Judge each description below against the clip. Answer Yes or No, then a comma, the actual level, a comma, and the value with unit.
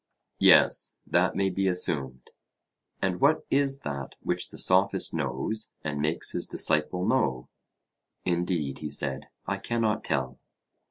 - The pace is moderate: No, slow, 130 wpm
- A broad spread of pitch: Yes, wide, 6.0 semitones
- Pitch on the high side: No, very low, 85 Hz